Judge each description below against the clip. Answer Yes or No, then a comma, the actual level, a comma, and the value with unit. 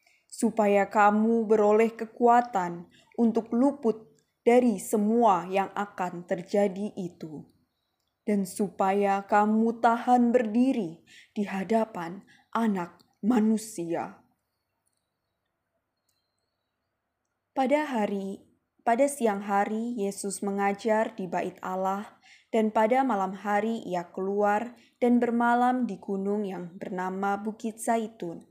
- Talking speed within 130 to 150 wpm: No, average, 95 wpm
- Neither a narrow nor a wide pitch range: Yes, average, 3.8 semitones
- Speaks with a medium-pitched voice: No, high, 205 Hz